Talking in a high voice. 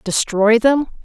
Yes: high, 230 Hz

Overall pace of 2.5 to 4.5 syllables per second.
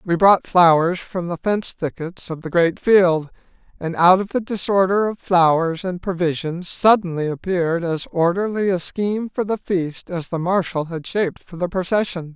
No: 4.8 syllables/s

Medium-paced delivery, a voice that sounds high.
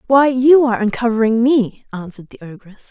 Yes: average, 165 wpm; high, 235 Hz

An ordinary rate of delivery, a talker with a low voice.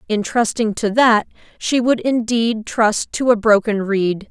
No: average, 165 wpm; high, 225 Hz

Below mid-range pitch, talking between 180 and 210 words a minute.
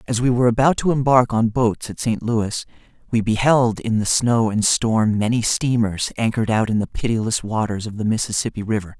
Yes: low, 115 Hz; average, 200 wpm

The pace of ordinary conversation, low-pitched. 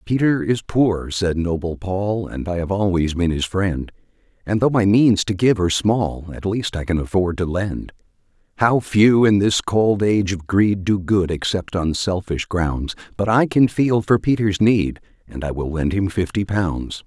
Yes: average, 195 wpm; very low, 95 Hz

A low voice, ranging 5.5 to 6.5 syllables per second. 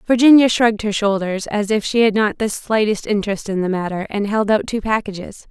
No: high, 210 Hz; 5.6 syllables/s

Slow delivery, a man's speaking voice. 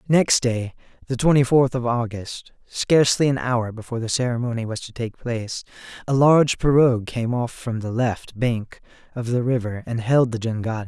No: average, 180 wpm; male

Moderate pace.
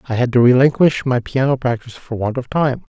No: fast, 225 wpm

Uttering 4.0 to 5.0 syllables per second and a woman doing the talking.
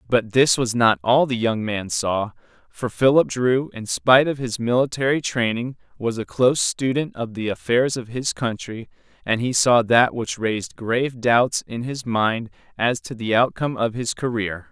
No: 4.6 syllables/s; male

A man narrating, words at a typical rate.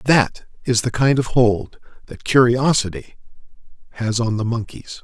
Yes: male; average, 145 wpm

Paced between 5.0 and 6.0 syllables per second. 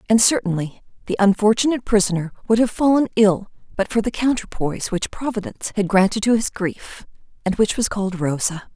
Yes: 5.8 syllables/s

